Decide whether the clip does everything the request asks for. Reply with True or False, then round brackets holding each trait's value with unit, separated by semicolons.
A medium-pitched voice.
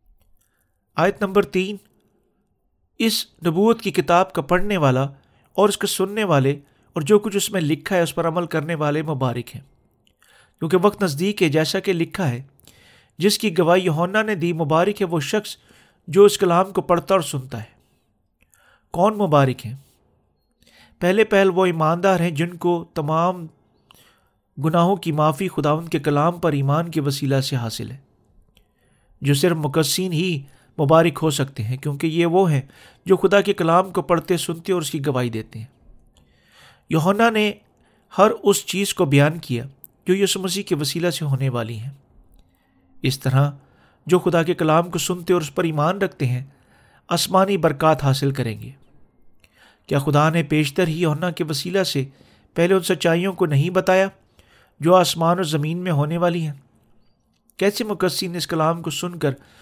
True (165 Hz)